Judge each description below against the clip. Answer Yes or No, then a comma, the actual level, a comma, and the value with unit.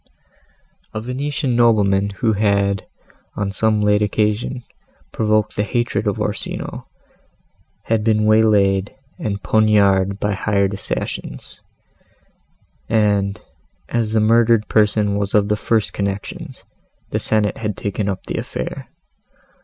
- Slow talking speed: Yes, slow, 120 wpm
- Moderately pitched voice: No, low, 105 Hz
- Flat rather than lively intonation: Yes, narrow, 1.7 semitones